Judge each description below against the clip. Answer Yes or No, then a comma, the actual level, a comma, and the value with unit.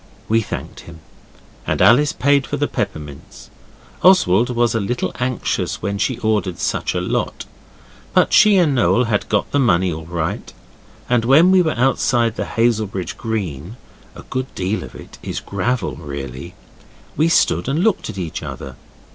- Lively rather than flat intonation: Yes, wide, 6.5 semitones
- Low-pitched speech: Yes, low, 115 Hz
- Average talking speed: Yes, average, 165 wpm